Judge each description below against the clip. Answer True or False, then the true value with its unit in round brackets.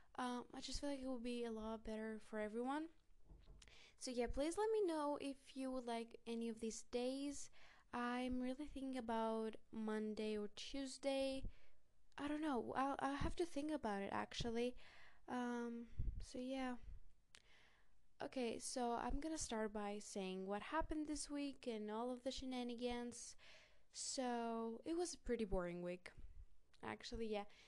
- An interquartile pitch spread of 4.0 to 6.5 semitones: False (3.4 semitones)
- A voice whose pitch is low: False (245 Hz)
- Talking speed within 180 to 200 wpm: False (160 wpm)